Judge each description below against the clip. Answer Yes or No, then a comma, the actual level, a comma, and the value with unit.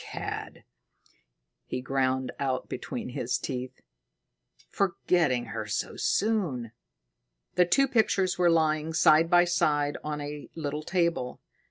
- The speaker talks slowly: Yes, slow, 120 wpm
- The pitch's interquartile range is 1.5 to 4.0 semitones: No, average, 4.9 semitones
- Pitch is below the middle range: No, medium, 155 Hz